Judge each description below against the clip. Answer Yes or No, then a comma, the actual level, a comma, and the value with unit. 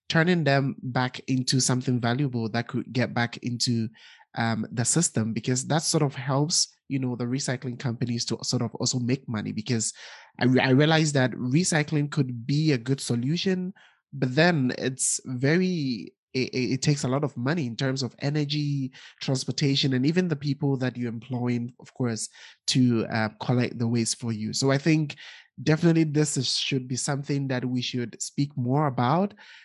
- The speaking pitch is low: Yes, low, 130 Hz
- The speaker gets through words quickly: No, average, 180 wpm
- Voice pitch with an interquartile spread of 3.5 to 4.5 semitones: No, average, 3.1 semitones